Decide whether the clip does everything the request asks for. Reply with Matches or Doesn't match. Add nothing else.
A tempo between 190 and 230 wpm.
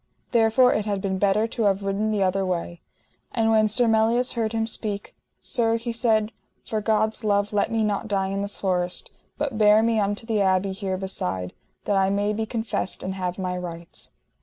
Matches